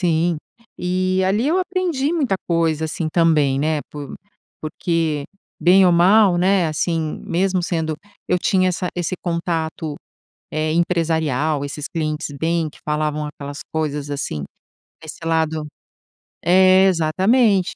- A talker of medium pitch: Yes, medium, 165 Hz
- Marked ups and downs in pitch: No, average, 3.1 semitones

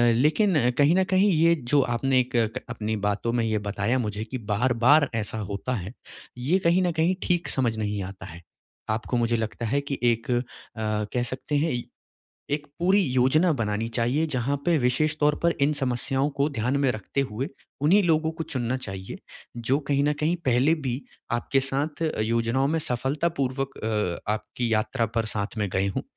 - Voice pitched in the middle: No, low, 125 Hz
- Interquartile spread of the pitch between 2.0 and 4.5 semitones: No, average, 4.9 semitones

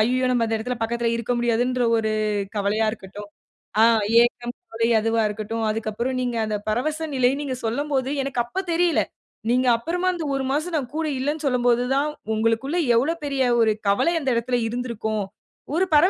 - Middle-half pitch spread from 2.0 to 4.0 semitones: Yes, average, 3.7 semitones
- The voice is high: Yes, high, 245 Hz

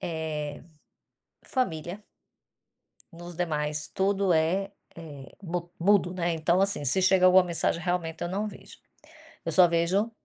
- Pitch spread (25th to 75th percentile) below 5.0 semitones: Yes, average, 2.7 semitones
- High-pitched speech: No, medium, 175 Hz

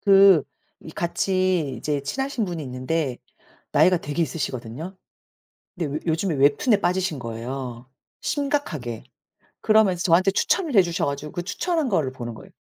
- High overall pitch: No, medium, 165 Hz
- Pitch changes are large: Yes, wide, 6.0 semitones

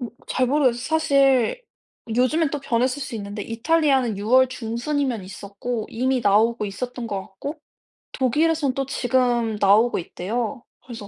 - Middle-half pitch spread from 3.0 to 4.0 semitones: Yes, average, 3.4 semitones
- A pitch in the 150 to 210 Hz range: No, high, 245 Hz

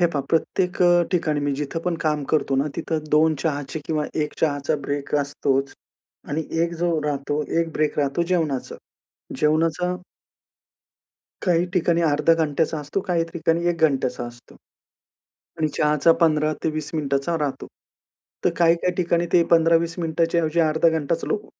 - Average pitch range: No, narrow, 2.3 semitones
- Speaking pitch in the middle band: Yes, medium, 160 Hz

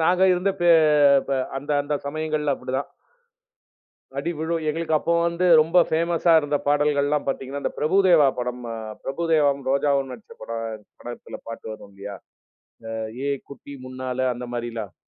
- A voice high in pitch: No, medium, 145 Hz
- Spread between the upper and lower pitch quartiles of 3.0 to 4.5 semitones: Yes, average, 3.9 semitones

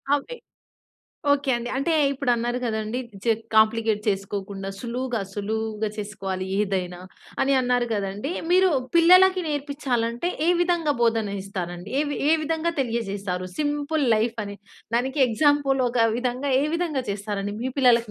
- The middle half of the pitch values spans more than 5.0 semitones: Yes, wide, 5.5 semitones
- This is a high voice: Yes, high, 235 Hz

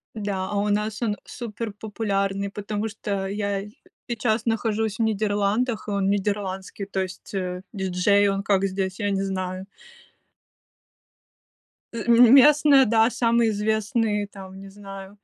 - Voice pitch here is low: No, high, 205 Hz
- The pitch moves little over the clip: Yes, narrow, 2.1 semitones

